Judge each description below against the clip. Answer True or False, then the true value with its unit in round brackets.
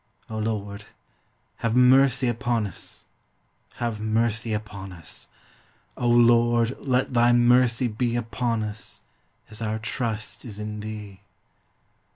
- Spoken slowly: True (120 wpm)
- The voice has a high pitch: False (115 Hz)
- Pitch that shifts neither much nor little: False (2.0 semitones)